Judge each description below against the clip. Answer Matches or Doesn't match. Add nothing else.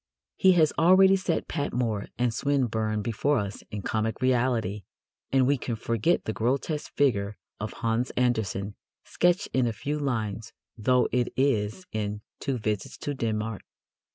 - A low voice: Matches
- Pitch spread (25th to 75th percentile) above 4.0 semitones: Matches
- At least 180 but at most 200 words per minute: Doesn't match